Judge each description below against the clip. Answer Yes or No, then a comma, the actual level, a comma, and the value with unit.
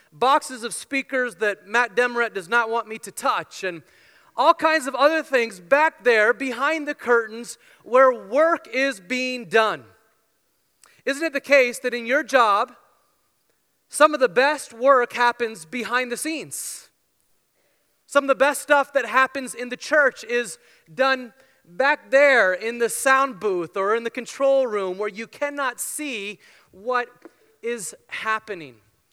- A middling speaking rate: Yes, average, 155 wpm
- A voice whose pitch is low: No, very high, 250 Hz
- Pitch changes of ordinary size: Yes, average, 3.3 semitones